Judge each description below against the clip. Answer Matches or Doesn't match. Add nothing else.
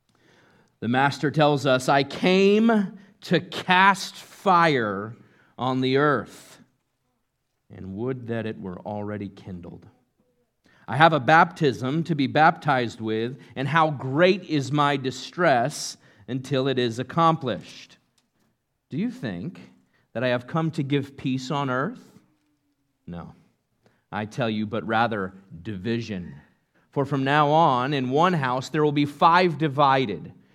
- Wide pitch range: Doesn't match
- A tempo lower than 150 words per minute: Matches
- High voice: Doesn't match